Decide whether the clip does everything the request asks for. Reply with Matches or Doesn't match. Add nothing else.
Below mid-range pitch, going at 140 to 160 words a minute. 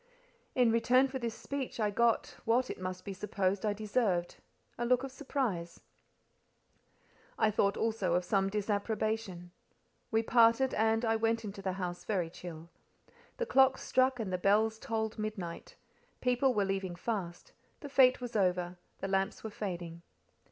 Doesn't match